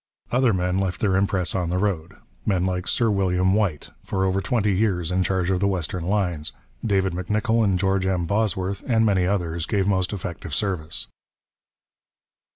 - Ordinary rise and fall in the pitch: No, narrow, 2.0 semitones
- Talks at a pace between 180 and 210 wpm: No, average, 170 wpm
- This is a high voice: No, very low, 95 Hz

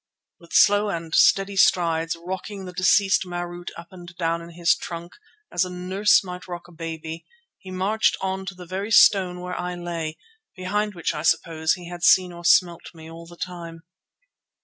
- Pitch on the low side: No, medium, 175 Hz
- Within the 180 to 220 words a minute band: Yes, average, 185 wpm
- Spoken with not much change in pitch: Yes, narrow, 1.9 semitones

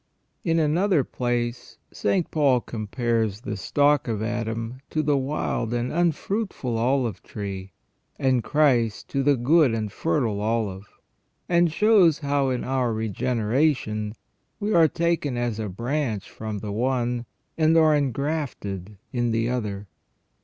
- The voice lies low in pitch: Yes, low, 125 Hz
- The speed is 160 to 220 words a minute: No, slow, 135 wpm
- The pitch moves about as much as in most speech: Yes, average, 5.0 semitones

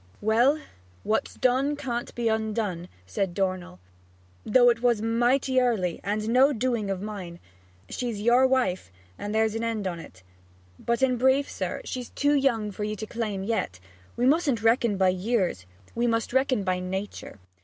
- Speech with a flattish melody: No, average, 4.1 semitones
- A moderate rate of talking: Yes, average, 165 wpm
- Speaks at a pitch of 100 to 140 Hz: No, high, 225 Hz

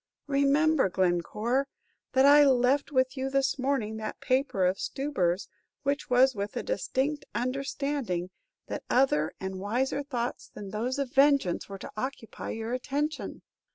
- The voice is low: No, very high, 260 Hz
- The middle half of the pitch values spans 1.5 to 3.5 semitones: No, average, 4.7 semitones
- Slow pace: No, average, 145 wpm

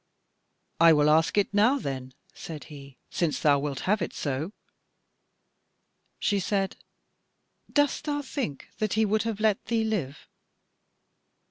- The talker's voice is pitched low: No, high, 190 Hz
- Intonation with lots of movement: Yes, wide, 6.8 semitones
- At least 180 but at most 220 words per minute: No, slow, 135 wpm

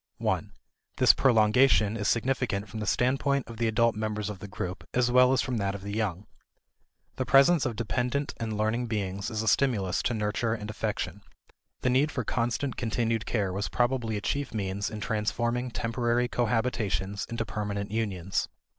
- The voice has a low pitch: Yes, low, 115 Hz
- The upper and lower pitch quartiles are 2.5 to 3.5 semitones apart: Yes, average, 2.9 semitones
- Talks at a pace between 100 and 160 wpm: No, average, 175 wpm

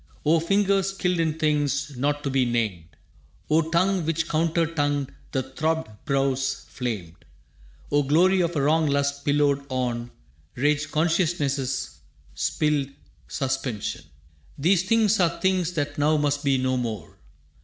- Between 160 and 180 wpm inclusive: No, slow, 135 wpm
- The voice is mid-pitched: Yes, medium, 145 Hz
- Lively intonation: No, average, 3.6 semitones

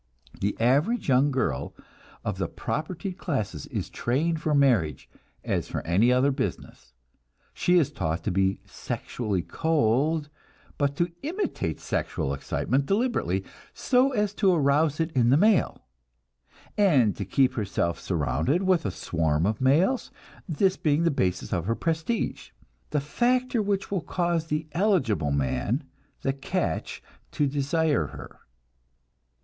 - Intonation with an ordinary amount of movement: No, wide, 8.1 semitones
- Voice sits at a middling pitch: Yes, medium, 145 Hz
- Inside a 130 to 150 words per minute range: Yes, average, 140 wpm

